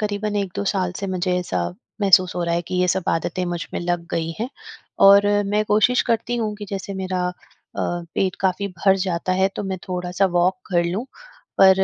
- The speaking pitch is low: No, medium, 185 Hz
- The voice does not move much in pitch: Yes, narrow, 2.2 semitones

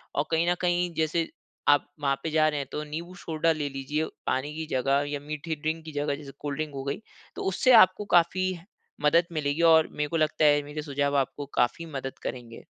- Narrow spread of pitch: Yes, narrow, 2.2 semitones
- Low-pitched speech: No, medium, 150 Hz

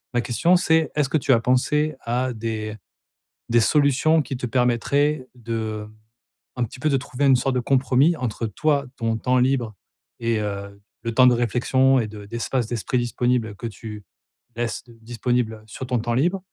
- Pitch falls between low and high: No, low, 125 Hz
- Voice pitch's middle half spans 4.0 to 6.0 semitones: No, average, 3.0 semitones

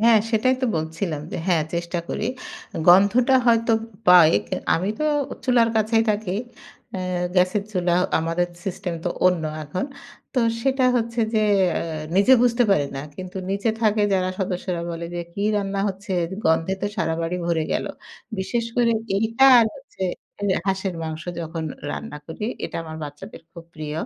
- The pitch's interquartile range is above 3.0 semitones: Yes, average, 4.9 semitones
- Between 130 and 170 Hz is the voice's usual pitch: No, high, 190 Hz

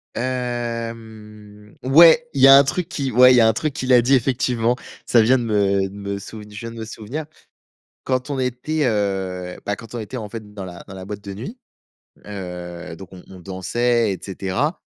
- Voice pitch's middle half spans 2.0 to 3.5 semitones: No, average, 4.2 semitones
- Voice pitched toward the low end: Yes, low, 115 Hz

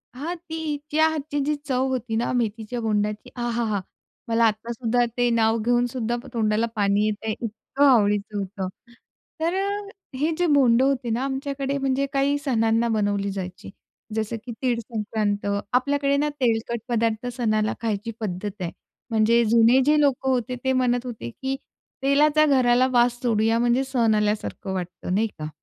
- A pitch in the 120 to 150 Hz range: No, high, 235 Hz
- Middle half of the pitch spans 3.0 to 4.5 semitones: Yes, average, 3.6 semitones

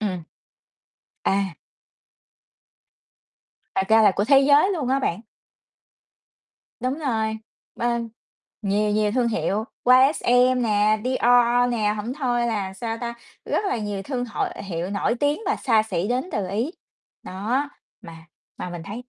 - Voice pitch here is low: No, high, 225 Hz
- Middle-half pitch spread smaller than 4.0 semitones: Yes, average, 3.4 semitones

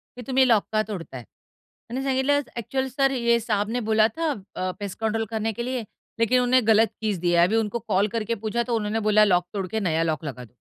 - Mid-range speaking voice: No, high, 220 Hz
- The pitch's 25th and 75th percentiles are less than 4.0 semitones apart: Yes, average, 3.4 semitones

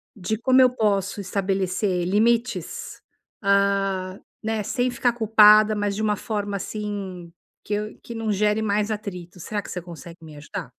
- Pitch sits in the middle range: No, high, 205 Hz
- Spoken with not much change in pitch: Yes, narrow, 2.3 semitones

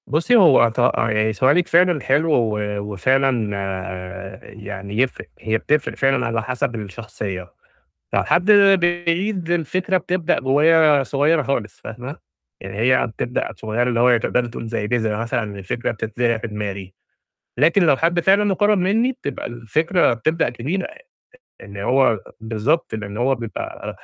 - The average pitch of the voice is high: No, low, 125 Hz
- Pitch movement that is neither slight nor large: No, wide, 7.3 semitones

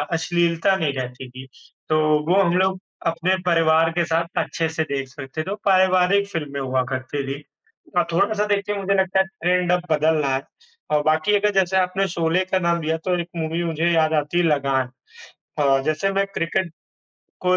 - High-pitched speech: No, medium, 170 Hz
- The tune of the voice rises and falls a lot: No, average, 3.3 semitones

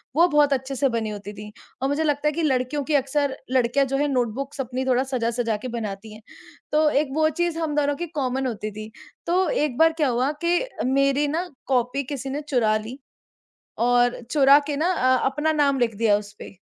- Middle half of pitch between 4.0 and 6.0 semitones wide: No, average, 3.5 semitones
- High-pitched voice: Yes, very high, 265 Hz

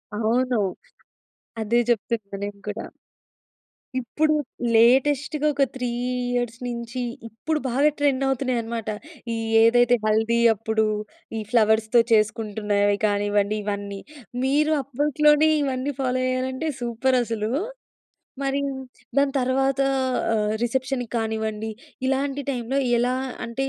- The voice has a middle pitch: No, high, 240 Hz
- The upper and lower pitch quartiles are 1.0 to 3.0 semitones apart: No, average, 3.5 semitones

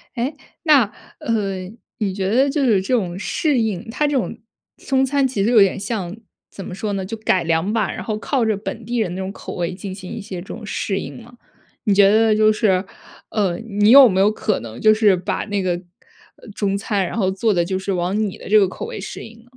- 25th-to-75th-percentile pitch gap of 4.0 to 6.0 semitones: No, average, 3.3 semitones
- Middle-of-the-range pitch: No, high, 205 Hz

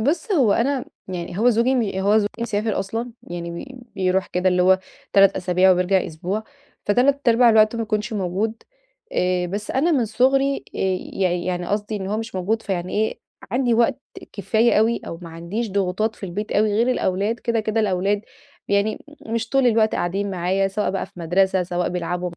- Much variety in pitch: No, average, 3.7 semitones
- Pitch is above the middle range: Yes, high, 205 Hz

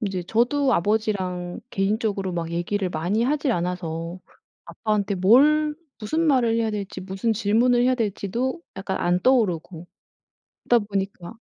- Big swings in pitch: No, average, 4.6 semitones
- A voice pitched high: Yes, high, 205 Hz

